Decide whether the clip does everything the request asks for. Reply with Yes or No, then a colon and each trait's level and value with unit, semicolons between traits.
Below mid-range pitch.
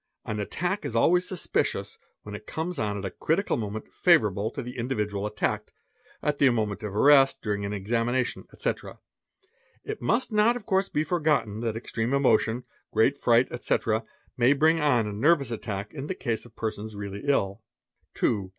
Yes: low, 120 Hz